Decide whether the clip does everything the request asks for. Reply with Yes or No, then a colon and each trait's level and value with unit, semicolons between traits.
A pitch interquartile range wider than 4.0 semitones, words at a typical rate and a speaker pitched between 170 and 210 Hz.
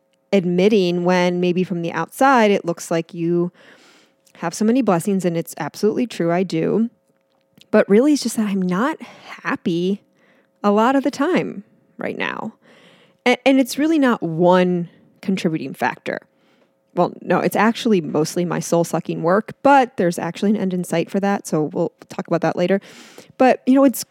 Yes: average, 4.5 semitones; average, 175 wpm; high, 190 Hz